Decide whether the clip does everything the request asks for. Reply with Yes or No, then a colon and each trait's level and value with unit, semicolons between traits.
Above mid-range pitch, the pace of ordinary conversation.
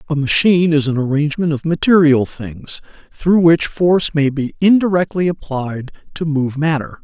No: medium, 155 Hz; average, 155 wpm